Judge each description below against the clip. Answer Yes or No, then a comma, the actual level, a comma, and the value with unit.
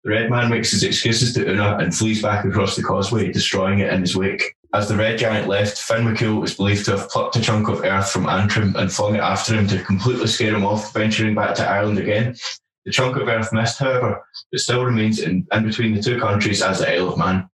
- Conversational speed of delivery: No, fast, 245 wpm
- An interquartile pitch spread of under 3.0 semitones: Yes, narrow, 2.4 semitones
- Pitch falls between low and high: No, low, 105 Hz